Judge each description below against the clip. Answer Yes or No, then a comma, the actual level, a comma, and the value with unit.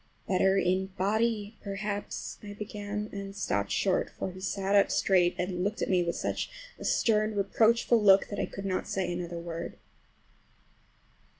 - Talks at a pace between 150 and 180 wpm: Yes, average, 160 wpm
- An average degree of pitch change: No, narrow, 2.1 semitones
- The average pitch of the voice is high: Yes, high, 195 Hz